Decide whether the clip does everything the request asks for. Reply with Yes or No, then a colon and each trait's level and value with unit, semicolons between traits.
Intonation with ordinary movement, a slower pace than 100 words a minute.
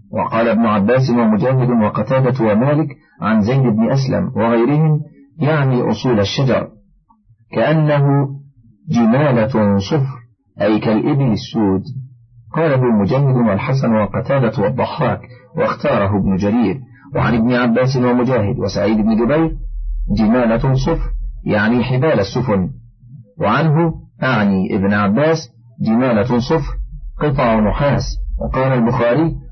No: average, 4.2 semitones; average, 105 wpm